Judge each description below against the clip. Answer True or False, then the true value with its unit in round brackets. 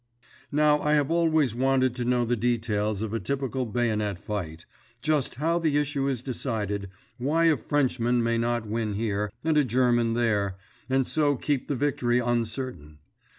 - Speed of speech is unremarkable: True (160 wpm)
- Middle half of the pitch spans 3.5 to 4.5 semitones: True (4.0 semitones)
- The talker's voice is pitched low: True (120 Hz)